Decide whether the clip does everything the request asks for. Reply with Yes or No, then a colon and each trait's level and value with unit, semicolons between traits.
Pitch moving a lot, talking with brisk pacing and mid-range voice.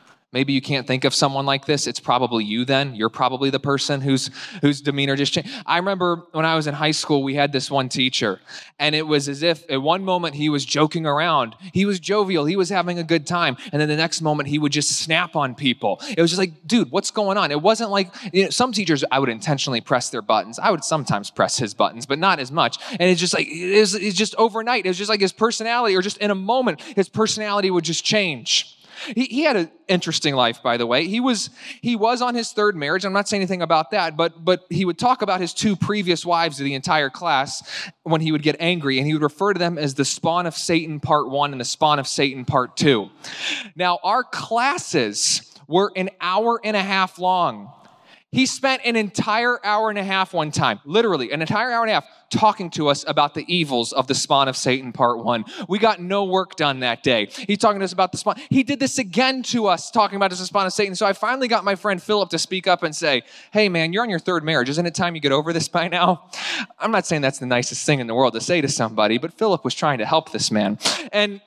Yes: wide, 6.1 semitones; fast, 250 wpm; medium, 170 Hz